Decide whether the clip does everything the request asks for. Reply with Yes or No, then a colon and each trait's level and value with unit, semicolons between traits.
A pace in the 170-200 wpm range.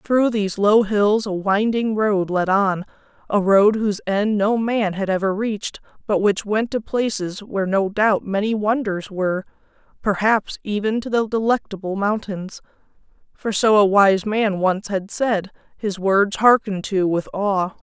No: average, 160 wpm